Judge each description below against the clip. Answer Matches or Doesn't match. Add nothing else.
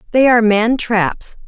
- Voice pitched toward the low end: Doesn't match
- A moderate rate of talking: Matches